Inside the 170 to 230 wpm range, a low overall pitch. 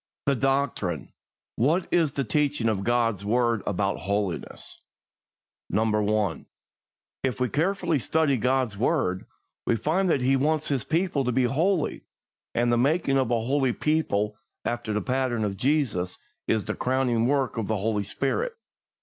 No: average, 155 wpm; low, 125 Hz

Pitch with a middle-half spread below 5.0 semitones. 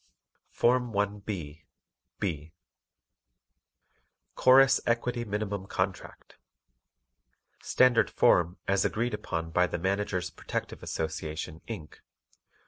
No: wide, 5.5 semitones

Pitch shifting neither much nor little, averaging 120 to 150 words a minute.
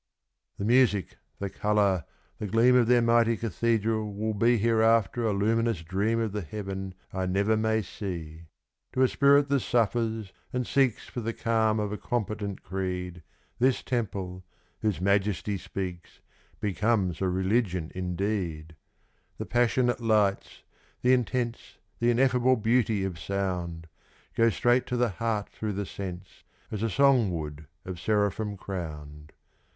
Yes: average, 3.7 semitones; average, 145 wpm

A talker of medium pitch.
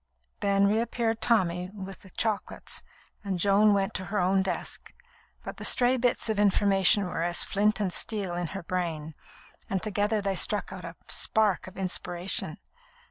No: high, 195 Hz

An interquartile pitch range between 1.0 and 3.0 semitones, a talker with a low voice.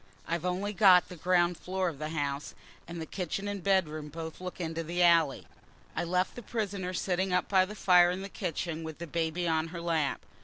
No: narrow, 2.4 semitones; medium, 175 Hz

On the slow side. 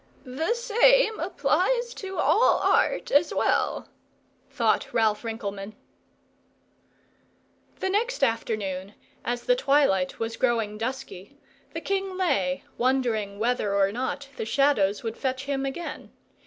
Yes: slow, 120 wpm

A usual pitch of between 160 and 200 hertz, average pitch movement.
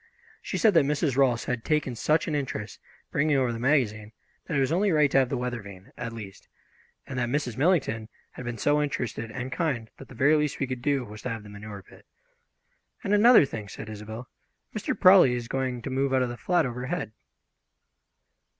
No: low, 130 Hz; average, 4.4 semitones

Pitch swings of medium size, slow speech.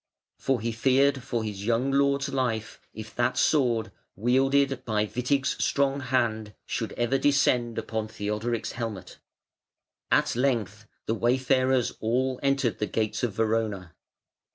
Yes: average, 3.4 semitones; slow, 130 wpm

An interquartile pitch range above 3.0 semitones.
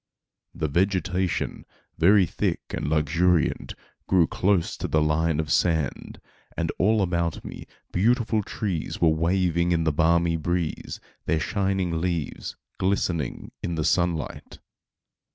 No: average, 2.7 semitones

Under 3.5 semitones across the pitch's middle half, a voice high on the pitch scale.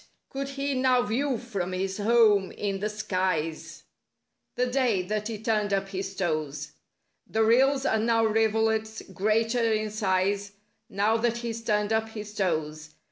Yes: average, 2.9 semitones; high, 215 Hz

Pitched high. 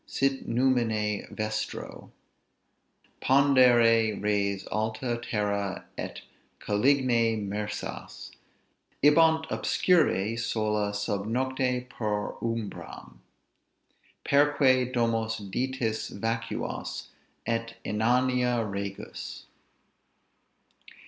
No: low, 115 Hz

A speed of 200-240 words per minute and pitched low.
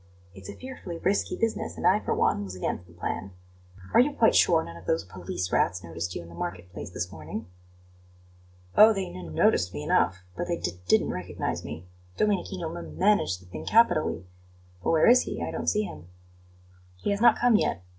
Yes: fast, 205 wpm; very low, 95 Hz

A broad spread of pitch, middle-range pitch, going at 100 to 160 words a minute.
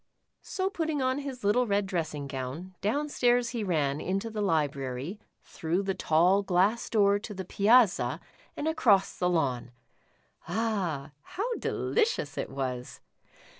No: wide, 7.0 semitones; high, 195 Hz; average, 140 wpm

